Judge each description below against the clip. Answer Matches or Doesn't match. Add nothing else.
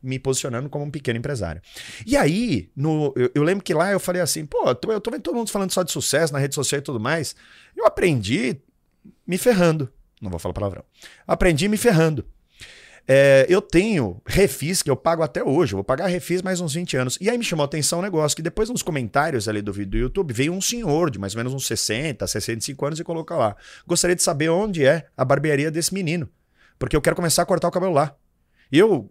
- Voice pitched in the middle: Matches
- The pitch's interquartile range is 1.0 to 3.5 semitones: Doesn't match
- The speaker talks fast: Matches